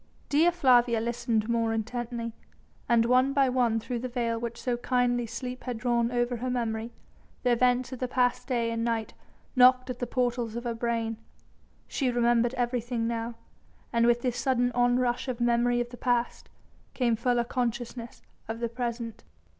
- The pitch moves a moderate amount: No, narrow, 1.2 semitones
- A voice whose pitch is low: No, high, 240 Hz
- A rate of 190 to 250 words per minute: No, average, 170 wpm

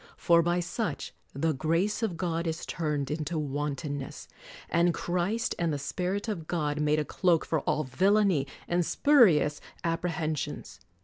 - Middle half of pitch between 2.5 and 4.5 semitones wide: Yes, average, 2.9 semitones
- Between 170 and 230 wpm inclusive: No, average, 145 wpm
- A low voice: No, medium, 165 Hz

